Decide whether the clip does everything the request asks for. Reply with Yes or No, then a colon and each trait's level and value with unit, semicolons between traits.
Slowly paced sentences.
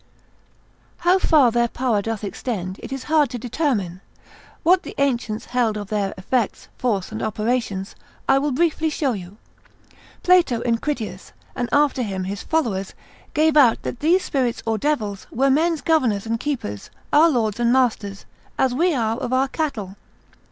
No: average, 165 wpm